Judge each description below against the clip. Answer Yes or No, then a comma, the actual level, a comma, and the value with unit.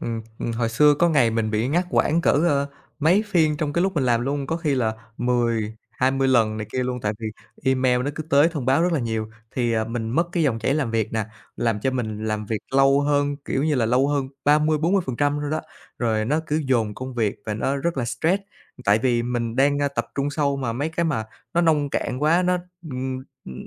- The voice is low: Yes, low, 130 Hz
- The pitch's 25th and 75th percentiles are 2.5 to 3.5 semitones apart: No, average, 4.3 semitones